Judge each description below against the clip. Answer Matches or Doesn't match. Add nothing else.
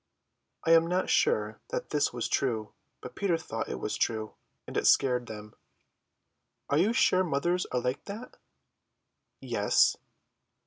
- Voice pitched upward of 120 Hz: Matches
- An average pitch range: Doesn't match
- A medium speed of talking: Matches